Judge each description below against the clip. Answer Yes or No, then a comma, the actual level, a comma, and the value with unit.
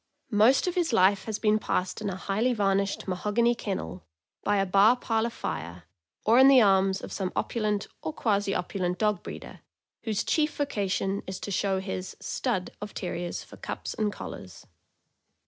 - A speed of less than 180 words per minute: No, average, 185 wpm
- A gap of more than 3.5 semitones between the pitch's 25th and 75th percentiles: No, average, 2.7 semitones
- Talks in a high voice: Yes, high, 200 Hz